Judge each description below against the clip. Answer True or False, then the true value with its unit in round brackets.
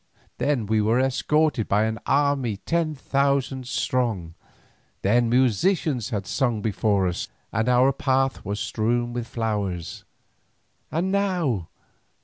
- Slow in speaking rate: True (125 wpm)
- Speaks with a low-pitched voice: True (120 Hz)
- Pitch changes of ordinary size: True (4.3 semitones)